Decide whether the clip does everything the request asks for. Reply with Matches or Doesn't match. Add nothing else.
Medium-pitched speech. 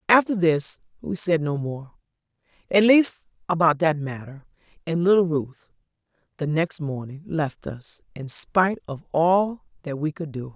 Matches